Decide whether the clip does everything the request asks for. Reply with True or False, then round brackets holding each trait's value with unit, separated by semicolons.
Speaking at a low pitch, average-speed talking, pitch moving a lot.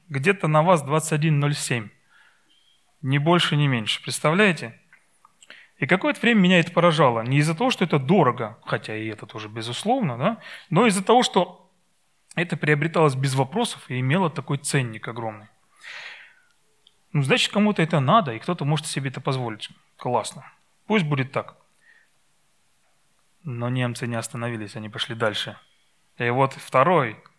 False (150 Hz; 140 wpm; 6.8 semitones)